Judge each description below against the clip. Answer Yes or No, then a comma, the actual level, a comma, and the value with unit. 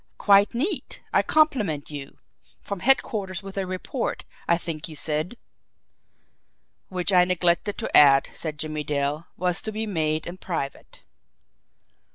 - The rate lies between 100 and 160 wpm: Yes, average, 140 wpm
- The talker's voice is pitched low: No, medium, 180 Hz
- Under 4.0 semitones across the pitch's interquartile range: No, average, 4.6 semitones